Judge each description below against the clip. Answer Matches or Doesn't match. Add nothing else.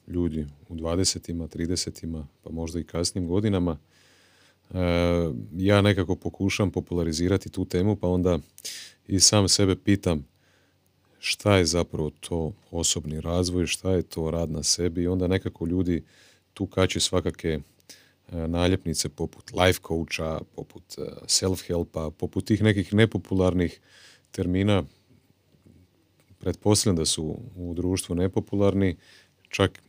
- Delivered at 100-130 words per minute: Matches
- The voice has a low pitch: Matches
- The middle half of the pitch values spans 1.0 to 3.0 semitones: Matches